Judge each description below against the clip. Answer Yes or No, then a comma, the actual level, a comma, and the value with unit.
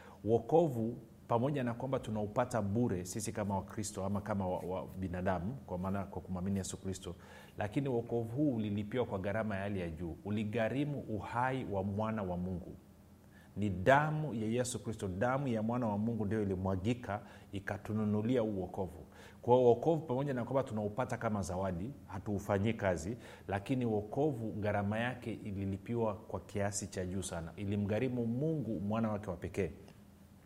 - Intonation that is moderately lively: Yes, average, 3.2 semitones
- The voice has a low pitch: Yes, low, 105 Hz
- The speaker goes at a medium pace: No, fast, 150 wpm